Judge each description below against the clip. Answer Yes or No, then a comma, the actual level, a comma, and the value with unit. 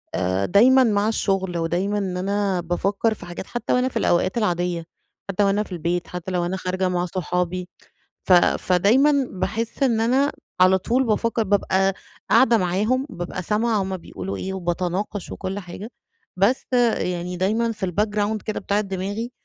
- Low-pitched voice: No, high, 195 Hz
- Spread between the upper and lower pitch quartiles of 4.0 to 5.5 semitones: No, average, 3.3 semitones